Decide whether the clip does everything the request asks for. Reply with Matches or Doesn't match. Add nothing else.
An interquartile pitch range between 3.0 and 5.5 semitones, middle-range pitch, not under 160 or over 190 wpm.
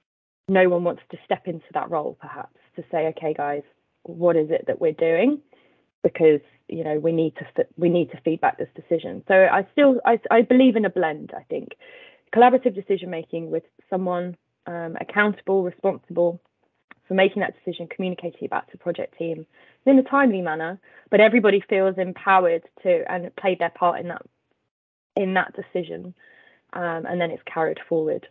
Matches